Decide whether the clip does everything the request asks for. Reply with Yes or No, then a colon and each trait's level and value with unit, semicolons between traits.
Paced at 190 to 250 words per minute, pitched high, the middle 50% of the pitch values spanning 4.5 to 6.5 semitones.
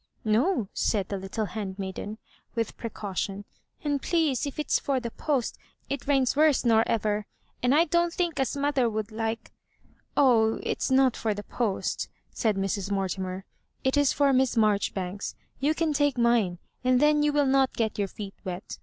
Yes: average, 200 wpm; high, 235 Hz; wide, 5.5 semitones